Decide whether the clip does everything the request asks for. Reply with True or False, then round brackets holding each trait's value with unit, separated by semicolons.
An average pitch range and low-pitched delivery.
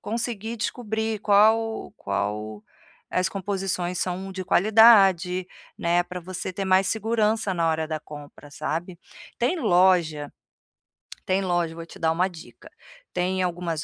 False (3.6 semitones; 185 Hz)